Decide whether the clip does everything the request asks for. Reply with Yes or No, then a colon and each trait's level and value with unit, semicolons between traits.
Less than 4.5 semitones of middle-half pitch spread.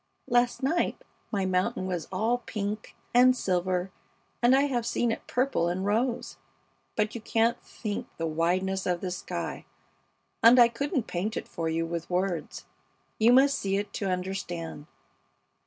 No: average, 4.8 semitones